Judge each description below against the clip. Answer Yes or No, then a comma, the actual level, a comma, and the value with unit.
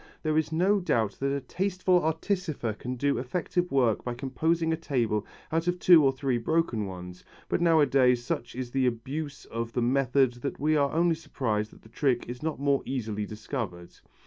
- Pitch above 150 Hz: No, low, 135 Hz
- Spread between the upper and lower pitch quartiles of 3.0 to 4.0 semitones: No, average, 5.1 semitones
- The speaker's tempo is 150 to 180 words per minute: No, average, 190 wpm